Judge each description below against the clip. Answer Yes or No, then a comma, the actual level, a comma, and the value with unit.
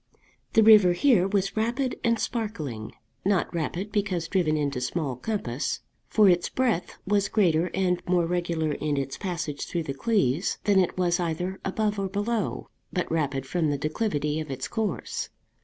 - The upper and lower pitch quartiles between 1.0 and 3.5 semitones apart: No, average, 5.0 semitones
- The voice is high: No, medium, 180 Hz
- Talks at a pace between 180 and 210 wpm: No, average, 165 wpm